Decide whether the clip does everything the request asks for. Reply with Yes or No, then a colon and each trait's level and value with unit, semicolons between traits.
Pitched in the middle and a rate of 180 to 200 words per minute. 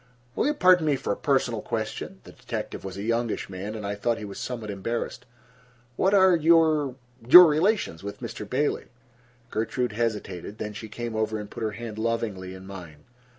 No: low, 115 Hz; average, 185 wpm